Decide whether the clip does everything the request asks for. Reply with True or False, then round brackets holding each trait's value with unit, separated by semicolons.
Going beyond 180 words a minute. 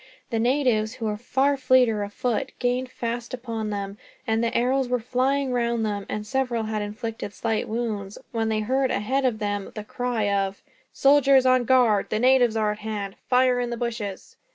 True (190 wpm)